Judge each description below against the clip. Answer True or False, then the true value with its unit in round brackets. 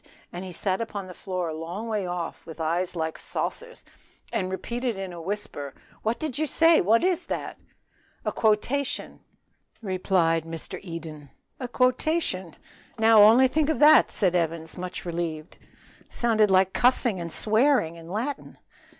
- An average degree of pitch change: False (6.0 semitones)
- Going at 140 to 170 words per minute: True (145 wpm)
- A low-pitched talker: False (190 Hz)